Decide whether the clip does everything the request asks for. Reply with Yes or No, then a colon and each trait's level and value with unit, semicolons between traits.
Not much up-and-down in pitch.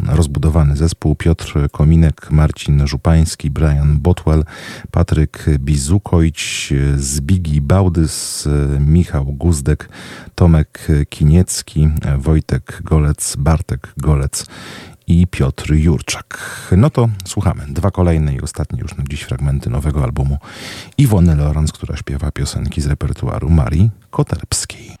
No: average, 3.6 semitones